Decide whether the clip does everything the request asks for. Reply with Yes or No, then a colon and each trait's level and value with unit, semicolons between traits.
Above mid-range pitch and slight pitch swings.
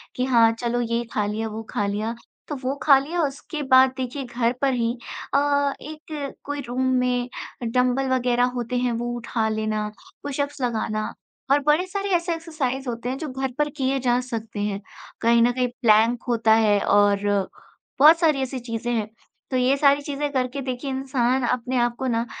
No: very high, 250 Hz; average, 3.0 semitones